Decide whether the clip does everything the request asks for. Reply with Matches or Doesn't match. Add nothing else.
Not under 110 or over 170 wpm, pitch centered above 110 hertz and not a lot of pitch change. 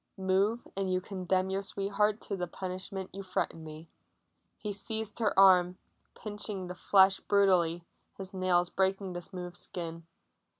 Matches